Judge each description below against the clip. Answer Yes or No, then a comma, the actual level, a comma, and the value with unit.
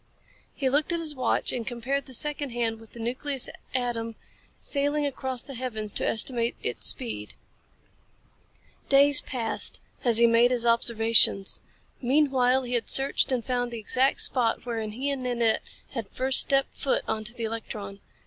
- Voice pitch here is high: Yes, high, 245 Hz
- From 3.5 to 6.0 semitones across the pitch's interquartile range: No, average, 2.8 semitones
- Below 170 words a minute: Yes, average, 160 wpm